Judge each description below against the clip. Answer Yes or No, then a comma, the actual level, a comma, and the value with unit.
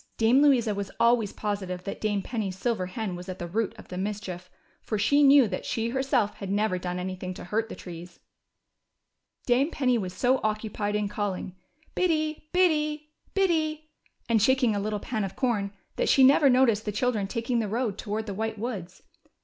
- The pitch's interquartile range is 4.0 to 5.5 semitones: Yes, average, 4.5 semitones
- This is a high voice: Yes, high, 215 Hz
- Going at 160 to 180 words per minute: No, average, 190 wpm